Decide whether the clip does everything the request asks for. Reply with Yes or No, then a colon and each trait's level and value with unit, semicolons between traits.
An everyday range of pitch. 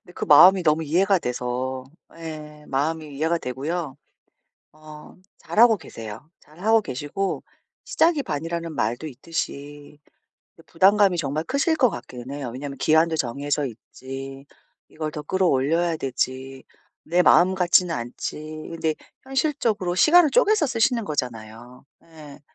Yes: average, 4.9 semitones